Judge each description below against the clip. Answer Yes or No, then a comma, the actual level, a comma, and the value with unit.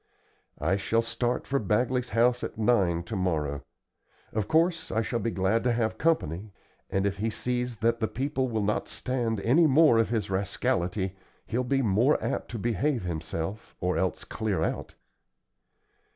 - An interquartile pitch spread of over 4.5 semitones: No, average, 4.2 semitones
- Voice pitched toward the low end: Yes, low, 115 Hz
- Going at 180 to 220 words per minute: No, average, 165 wpm